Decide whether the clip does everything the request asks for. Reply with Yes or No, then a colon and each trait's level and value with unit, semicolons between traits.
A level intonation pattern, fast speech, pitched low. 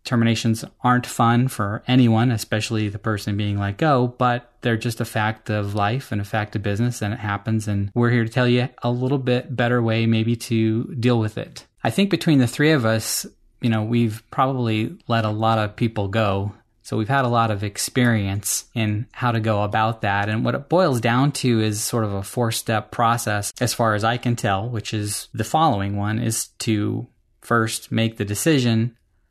Yes: narrow, 2.3 semitones; fast, 210 wpm; low, 115 Hz